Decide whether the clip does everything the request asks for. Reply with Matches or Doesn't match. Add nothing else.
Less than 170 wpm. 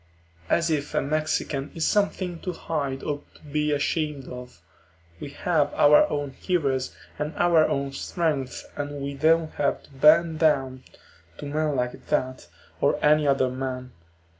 Matches